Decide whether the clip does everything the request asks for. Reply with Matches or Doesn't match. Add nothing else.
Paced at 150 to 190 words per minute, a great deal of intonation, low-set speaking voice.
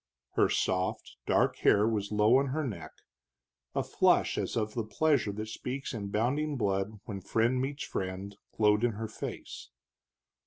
Doesn't match